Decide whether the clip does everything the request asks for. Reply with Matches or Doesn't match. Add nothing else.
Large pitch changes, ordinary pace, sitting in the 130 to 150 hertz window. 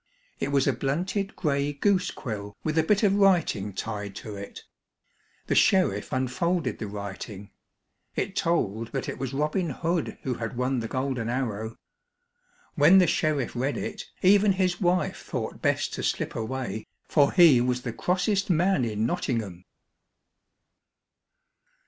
Matches